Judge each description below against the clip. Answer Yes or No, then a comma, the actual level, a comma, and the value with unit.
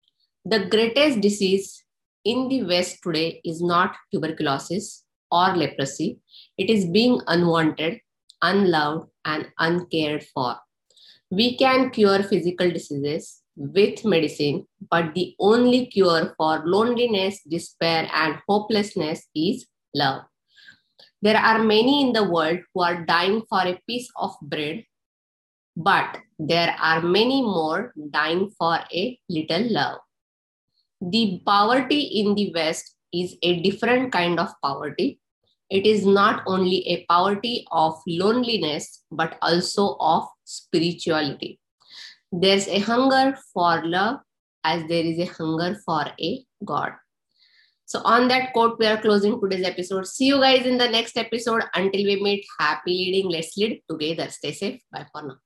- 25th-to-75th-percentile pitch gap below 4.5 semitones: No, average, 4.8 semitones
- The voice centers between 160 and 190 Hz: Yes, medium, 185 Hz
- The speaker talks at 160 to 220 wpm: No, slow, 135 wpm